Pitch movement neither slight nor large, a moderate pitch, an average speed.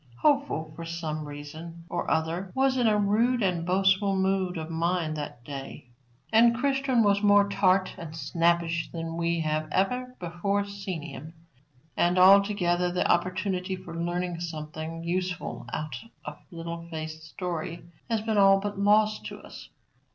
Yes: average, 3.5 semitones; medium, 180 Hz; average, 150 wpm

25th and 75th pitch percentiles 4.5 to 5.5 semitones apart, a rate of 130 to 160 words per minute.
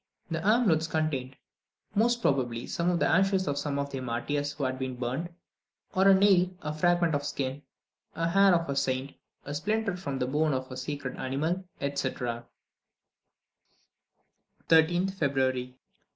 Yes: average, 4.9 semitones; average, 155 wpm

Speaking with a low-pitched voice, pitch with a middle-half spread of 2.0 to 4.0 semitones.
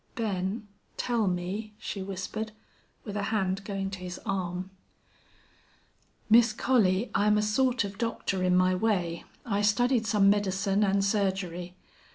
No: high, 200 Hz; narrow, 2.4 semitones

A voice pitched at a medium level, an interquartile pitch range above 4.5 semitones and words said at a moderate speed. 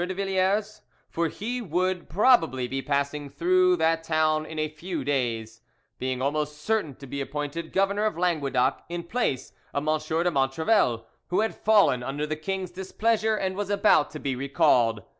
Yes: medium, 160 Hz; average, 5.2 semitones; average, 170 wpm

